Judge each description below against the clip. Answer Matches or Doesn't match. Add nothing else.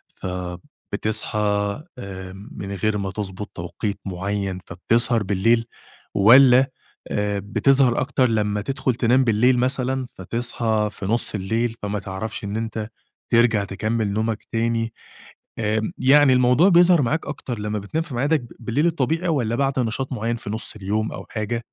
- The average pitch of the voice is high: Doesn't match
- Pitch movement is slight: Doesn't match